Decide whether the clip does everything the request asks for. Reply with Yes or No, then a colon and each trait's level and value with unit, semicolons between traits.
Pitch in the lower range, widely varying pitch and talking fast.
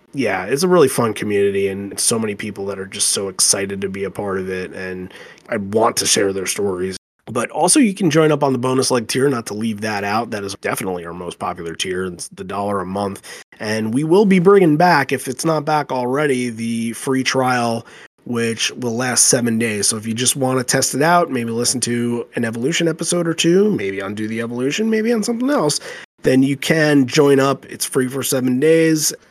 Yes: low, 120 Hz; wide, 6.2 semitones; fast, 225 wpm